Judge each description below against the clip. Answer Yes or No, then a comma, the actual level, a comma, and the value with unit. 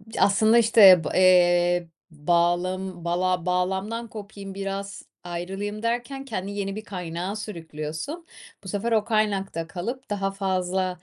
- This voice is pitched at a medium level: No, high, 195 Hz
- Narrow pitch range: No, average, 3.1 semitones